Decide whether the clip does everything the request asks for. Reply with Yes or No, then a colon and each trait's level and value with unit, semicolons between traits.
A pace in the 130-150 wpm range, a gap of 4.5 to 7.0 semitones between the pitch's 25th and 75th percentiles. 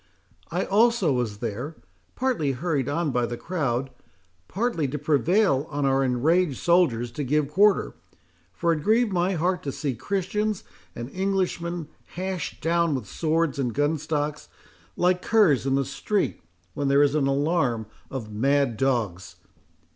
Yes: average, 145 wpm; average, 4.9 semitones